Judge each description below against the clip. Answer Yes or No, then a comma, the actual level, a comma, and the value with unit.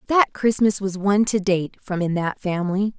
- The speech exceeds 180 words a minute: Yes, average, 200 wpm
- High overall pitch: Yes, high, 195 Hz